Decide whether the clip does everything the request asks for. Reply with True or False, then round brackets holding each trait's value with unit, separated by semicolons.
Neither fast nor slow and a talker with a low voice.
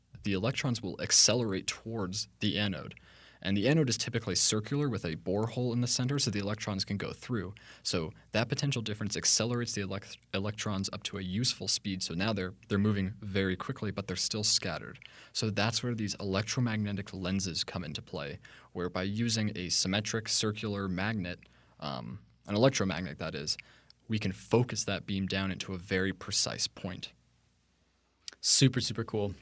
True (170 wpm; 105 Hz)